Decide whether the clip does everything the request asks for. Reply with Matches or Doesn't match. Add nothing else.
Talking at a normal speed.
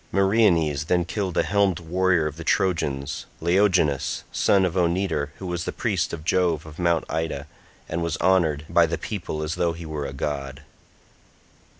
Matches